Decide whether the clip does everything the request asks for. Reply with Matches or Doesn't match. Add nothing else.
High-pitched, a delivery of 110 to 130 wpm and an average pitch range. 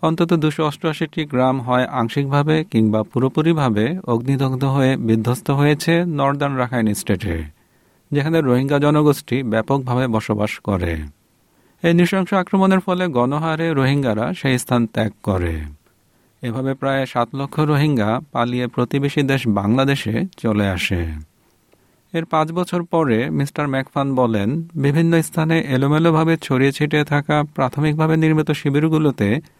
Doesn't match